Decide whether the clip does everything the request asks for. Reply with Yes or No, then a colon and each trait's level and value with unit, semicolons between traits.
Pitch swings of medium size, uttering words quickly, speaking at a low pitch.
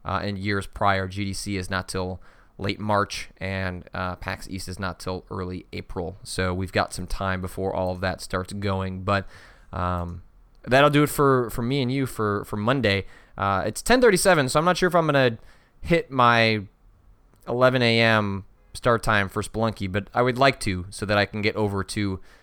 No: average, 3.6 semitones; average, 195 wpm; low, 100 Hz